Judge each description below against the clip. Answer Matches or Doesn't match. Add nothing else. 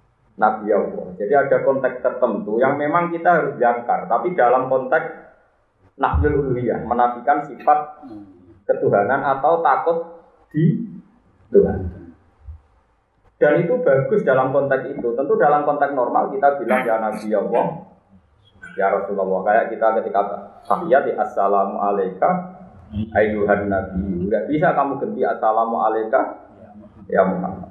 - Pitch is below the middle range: Matches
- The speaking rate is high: Doesn't match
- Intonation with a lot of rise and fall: Matches